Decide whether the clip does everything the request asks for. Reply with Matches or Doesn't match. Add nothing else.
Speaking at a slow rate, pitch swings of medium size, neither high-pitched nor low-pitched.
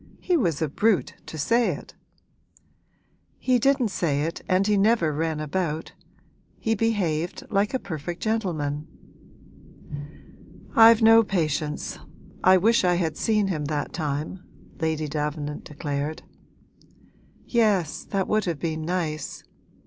Doesn't match